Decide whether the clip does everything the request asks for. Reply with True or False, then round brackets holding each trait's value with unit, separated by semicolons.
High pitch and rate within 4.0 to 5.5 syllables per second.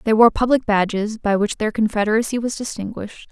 False (220 Hz; 6.0 syllables/s)